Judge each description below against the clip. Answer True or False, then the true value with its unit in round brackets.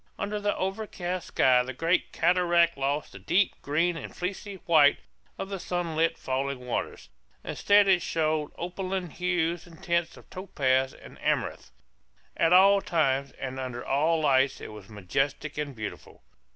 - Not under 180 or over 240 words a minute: False (150 wpm)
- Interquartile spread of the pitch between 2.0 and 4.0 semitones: False (4.8 semitones)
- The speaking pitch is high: False (165 Hz)